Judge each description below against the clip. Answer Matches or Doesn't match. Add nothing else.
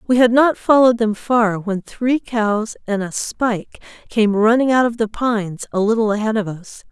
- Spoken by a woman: Matches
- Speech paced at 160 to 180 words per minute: Doesn't match